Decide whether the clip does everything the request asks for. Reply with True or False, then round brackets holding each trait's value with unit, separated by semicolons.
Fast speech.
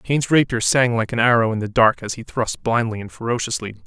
True (235 wpm)